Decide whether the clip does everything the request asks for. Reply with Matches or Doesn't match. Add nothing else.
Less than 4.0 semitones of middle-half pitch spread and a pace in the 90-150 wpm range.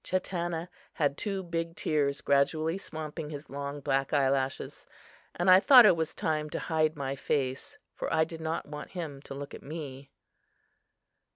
Doesn't match